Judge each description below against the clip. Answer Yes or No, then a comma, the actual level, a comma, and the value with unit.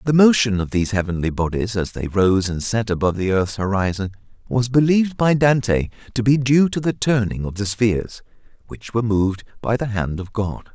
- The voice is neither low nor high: No, low, 110 Hz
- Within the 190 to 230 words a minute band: Yes, average, 200 wpm